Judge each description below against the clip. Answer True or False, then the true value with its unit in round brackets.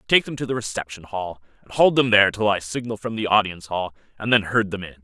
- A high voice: False (105 Hz)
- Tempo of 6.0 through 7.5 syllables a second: True (6.4 syllables/s)